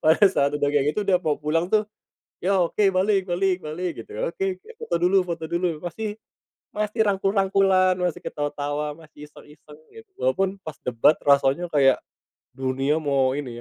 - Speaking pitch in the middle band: Yes, medium, 170 Hz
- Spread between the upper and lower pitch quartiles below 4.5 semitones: No, average, 4.8 semitones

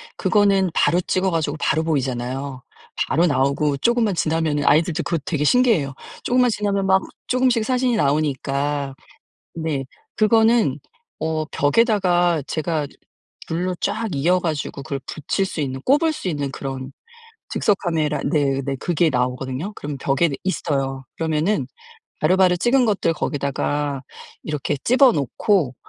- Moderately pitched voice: Yes, medium, 160 Hz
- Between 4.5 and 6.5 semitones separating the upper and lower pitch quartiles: Yes, wide, 5.6 semitones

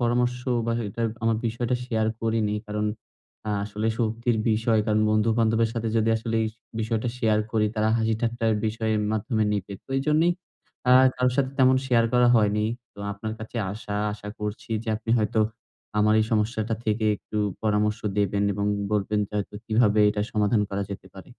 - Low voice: Yes, low, 110 Hz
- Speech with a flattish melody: Yes, narrow, 1.6 semitones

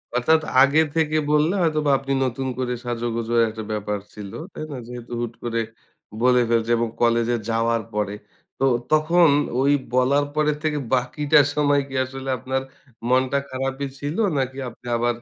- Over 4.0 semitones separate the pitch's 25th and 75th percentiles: No, average, 3.5 semitones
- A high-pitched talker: No, low, 130 Hz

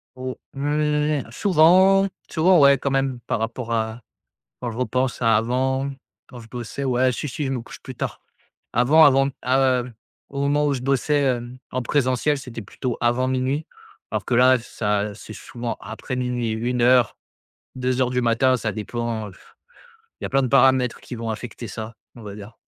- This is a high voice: No, low, 125 Hz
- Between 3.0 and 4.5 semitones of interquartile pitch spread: No, narrow, 2.6 semitones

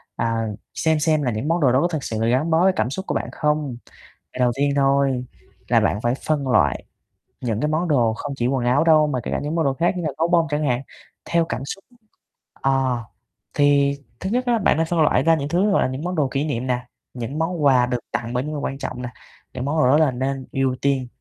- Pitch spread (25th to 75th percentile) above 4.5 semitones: No, average, 3.9 semitones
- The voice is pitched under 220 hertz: Yes, medium, 140 Hz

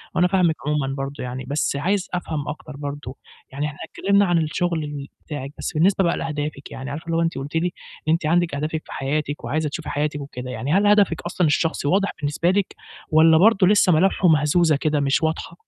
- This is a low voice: No, medium, 155 Hz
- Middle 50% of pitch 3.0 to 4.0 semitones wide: Yes, average, 3.3 semitones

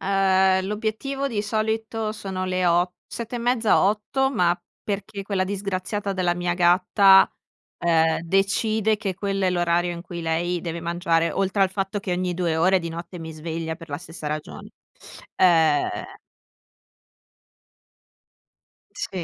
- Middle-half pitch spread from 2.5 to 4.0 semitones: Yes, average, 2.9 semitones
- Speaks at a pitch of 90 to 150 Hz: No, medium, 185 Hz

